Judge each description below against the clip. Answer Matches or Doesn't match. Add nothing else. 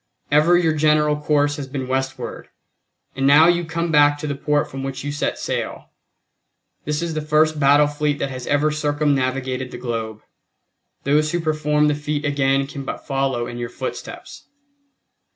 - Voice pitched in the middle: Matches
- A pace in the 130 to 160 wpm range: Doesn't match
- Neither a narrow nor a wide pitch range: Doesn't match